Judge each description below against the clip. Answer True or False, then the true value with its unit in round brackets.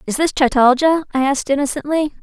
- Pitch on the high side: True (280 Hz)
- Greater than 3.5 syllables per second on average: True (6.5 syllables/s)